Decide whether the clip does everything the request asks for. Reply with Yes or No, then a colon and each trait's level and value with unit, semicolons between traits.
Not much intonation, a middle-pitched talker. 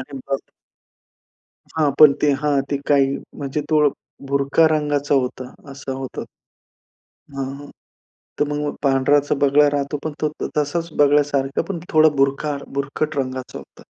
Yes: narrow, 1.4 semitones; medium, 145 Hz